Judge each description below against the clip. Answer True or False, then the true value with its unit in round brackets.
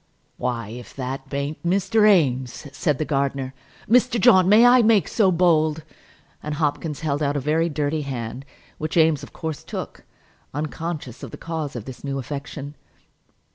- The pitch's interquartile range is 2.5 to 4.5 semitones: True (3.8 semitones)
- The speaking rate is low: False (165 wpm)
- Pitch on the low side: False (150 Hz)